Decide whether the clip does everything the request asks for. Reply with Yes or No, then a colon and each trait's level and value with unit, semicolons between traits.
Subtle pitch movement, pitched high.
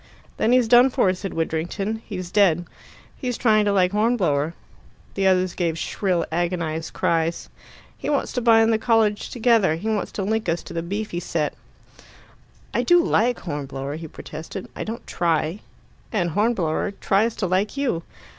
No: average, 4.8 semitones; high, 195 Hz